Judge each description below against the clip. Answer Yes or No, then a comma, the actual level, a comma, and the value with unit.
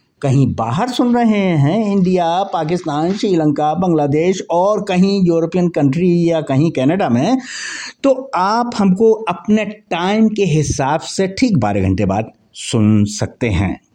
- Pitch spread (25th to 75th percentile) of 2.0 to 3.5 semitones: No, wide, 5.6 semitones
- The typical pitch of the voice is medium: Yes, medium, 175 Hz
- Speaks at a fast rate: No, average, 140 wpm